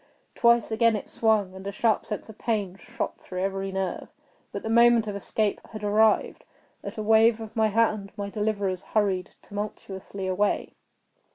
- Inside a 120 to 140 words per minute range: No, average, 170 wpm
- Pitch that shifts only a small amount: Yes, narrow, 2.1 semitones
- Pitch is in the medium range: No, high, 210 Hz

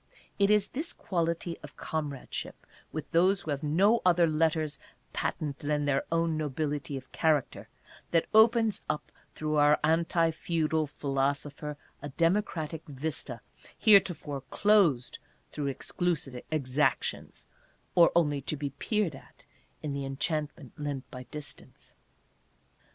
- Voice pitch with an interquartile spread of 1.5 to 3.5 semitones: Yes, average, 2.9 semitones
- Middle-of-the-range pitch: Yes, medium, 155 Hz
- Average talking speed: No, slow, 130 wpm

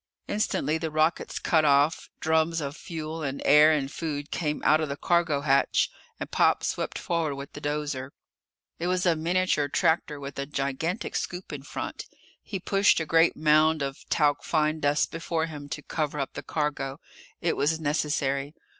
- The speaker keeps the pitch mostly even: Yes, narrow, 2.3 semitones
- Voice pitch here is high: No, medium, 155 Hz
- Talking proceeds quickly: No, average, 175 wpm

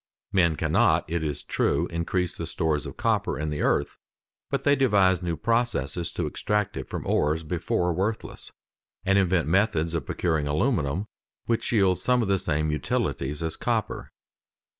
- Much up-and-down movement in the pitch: No, average, 4.0 semitones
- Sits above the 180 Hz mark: No, very low, 85 Hz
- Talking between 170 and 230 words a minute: No, average, 160 wpm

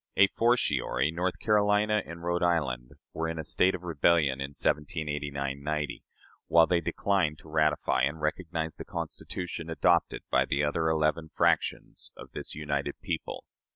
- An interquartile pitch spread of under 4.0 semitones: Yes, average, 2.9 semitones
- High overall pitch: No, very low, 80 Hz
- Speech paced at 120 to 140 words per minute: No, average, 155 wpm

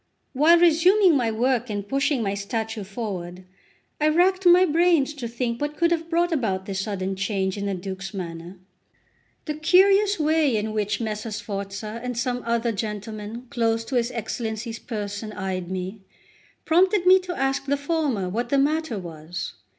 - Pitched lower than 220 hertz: No, high, 230 Hz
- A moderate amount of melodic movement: No, wide, 7.1 semitones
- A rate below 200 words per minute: Yes, average, 165 wpm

